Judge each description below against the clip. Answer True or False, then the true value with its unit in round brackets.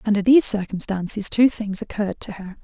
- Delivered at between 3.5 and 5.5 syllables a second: False (6.0 syllables/s)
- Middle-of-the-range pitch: False (205 Hz)